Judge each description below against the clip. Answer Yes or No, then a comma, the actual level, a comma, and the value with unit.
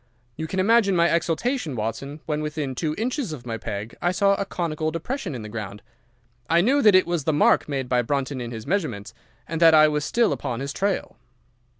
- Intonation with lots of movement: Yes, wide, 6.6 semitones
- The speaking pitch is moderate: Yes, medium, 155 Hz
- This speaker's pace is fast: Yes, fast, 215 wpm